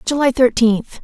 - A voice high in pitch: Yes, high, 245 Hz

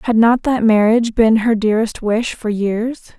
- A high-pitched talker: Yes, high, 225 Hz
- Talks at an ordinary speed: Yes, average, 190 wpm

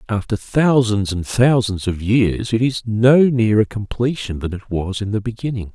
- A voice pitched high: No, low, 110 Hz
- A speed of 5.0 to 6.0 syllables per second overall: No, 4.5 syllables/s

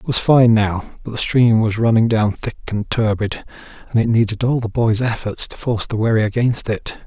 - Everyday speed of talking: No, fast, 220 wpm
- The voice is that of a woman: No, male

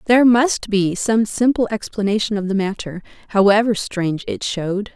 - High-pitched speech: Yes, high, 210 Hz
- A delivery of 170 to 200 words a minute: No, average, 155 wpm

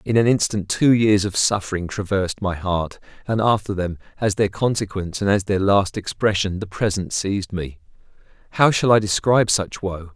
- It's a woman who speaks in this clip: No, male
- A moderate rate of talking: Yes, average, 185 wpm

